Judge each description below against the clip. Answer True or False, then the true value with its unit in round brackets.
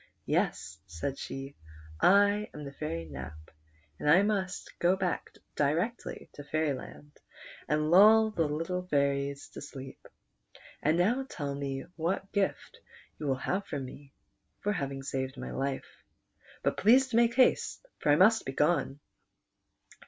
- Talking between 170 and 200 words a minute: False (150 wpm)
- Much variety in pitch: True (5.9 semitones)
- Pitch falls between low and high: True (150 Hz)